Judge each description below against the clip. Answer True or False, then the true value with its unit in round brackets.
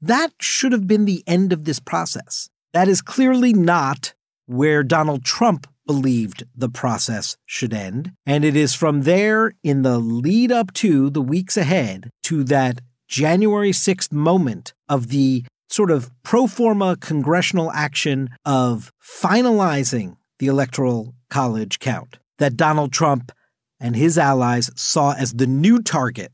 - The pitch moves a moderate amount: False (6.2 semitones)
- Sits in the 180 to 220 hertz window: False (145 Hz)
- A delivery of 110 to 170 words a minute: True (145 wpm)